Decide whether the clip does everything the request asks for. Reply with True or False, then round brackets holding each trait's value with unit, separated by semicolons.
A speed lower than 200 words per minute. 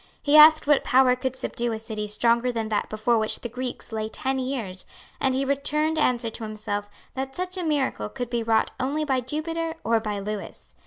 False (205 wpm)